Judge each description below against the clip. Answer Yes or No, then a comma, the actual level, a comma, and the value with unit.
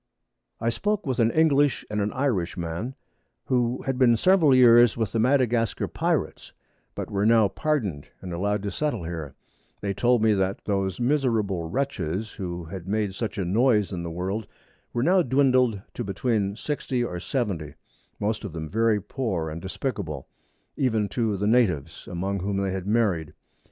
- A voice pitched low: Yes, low, 105 Hz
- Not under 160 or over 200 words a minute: Yes, average, 170 wpm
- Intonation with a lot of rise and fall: No, average, 4.7 semitones